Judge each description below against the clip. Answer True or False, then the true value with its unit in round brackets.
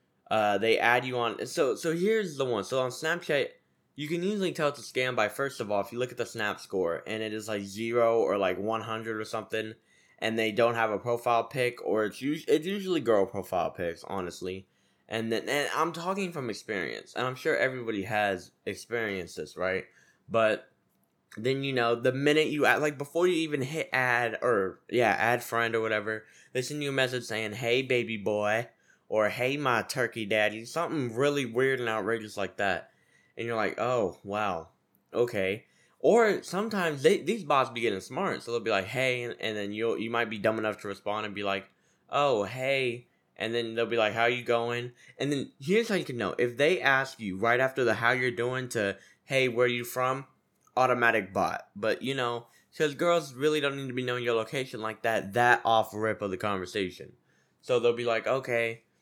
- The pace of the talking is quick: True (210 wpm)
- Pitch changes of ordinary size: True (3.2 semitones)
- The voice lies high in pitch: False (120 Hz)